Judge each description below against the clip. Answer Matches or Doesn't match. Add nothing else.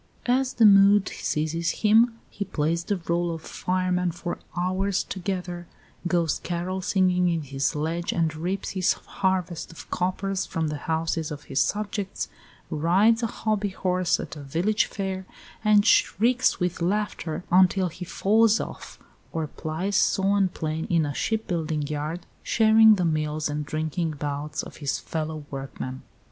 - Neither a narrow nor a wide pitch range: Matches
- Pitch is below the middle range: Doesn't match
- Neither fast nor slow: Matches